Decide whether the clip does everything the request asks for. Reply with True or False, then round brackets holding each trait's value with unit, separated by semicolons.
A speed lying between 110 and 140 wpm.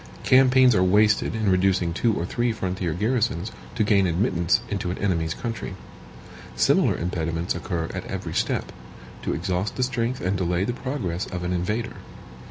False (165 wpm)